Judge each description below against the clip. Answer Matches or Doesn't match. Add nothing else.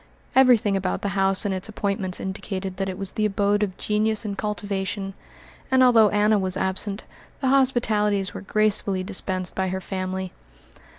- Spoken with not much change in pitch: Matches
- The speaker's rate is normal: Matches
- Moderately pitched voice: Doesn't match